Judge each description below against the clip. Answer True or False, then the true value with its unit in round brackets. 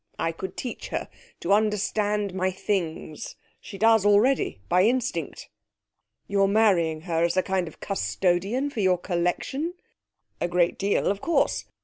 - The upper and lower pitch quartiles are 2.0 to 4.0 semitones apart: True (3.2 semitones)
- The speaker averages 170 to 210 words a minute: False (145 wpm)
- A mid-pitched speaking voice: False (195 Hz)